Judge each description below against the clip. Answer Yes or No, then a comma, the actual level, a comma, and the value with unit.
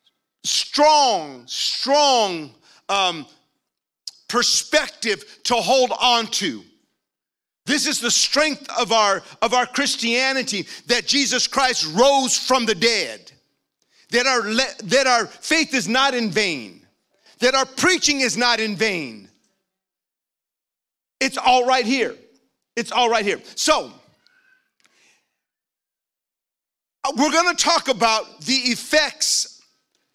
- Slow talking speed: Yes, slow, 115 wpm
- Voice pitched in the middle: No, very high, 255 Hz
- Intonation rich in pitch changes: No, average, 3.6 semitones